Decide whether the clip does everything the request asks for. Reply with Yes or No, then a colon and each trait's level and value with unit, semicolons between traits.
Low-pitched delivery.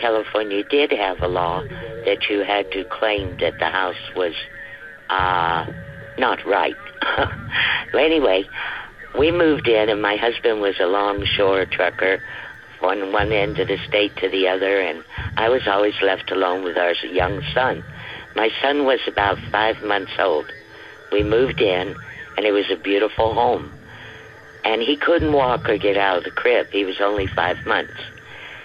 Yes: low, 100 Hz